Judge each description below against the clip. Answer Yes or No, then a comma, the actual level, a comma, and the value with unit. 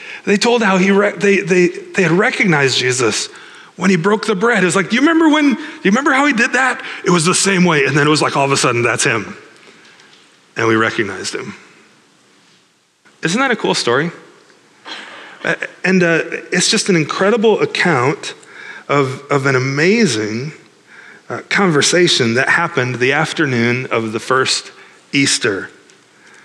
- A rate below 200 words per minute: Yes, average, 170 wpm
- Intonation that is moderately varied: No, wide, 8.8 semitones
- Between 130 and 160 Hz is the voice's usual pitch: No, medium, 185 Hz